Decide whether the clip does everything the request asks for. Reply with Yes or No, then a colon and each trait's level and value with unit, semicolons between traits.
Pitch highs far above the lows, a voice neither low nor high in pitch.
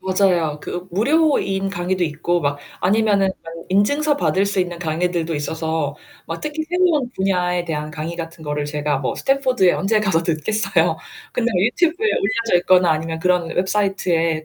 No: average, 4.6 semitones; medium, 180 Hz